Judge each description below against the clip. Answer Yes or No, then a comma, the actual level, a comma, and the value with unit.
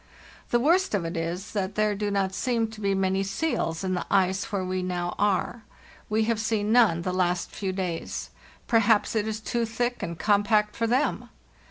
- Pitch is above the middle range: Yes, high, 205 Hz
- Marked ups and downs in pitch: No, average, 3.1 semitones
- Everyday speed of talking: Yes, average, 195 wpm